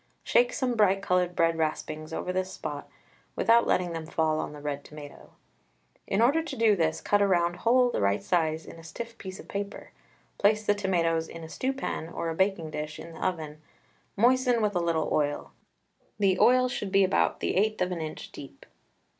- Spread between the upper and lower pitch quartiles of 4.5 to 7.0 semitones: Yes, average, 4.8 semitones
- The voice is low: No, medium, 180 Hz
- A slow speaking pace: No, fast, 205 wpm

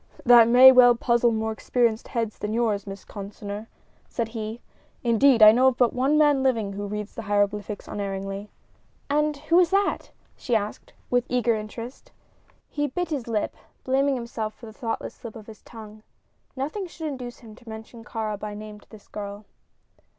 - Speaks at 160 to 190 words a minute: Yes, average, 180 wpm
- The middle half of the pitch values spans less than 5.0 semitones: Yes, average, 3.2 semitones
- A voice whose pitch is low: No, high, 230 Hz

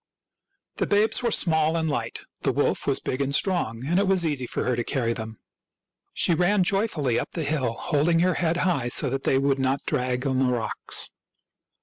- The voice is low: No, medium, 145 Hz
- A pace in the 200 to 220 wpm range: Yes, fast, 205 wpm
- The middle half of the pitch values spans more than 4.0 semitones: Yes, wide, 5.4 semitones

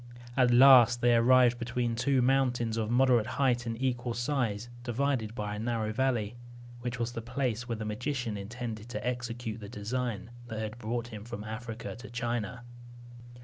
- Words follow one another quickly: No, average, 170 wpm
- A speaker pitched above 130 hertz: No, low, 120 Hz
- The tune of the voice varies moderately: No, narrow, 2.0 semitones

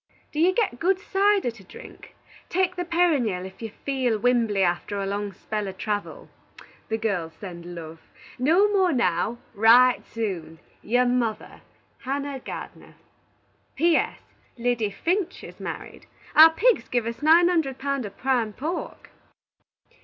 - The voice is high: Yes, high, 245 Hz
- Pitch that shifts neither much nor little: No, wide, 7.9 semitones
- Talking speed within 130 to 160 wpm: Yes, average, 145 wpm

